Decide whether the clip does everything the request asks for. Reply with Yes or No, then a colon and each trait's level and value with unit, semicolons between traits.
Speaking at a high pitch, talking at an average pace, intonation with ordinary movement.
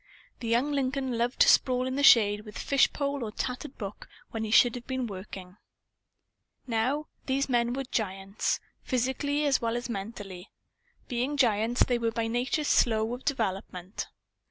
Yes: high, 240 Hz; average, 165 wpm; average, 3.3 semitones